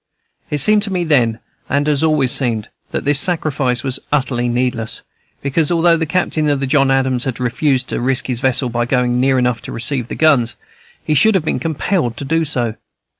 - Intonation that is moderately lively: Yes, average, 3.8 semitones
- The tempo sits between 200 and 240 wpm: Yes, fast, 205 wpm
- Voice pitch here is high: No, low, 135 Hz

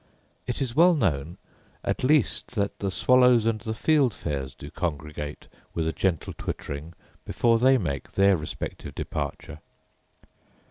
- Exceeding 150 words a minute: No, slow, 135 wpm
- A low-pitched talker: Yes, low, 100 Hz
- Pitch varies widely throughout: Yes, wide, 8.5 semitones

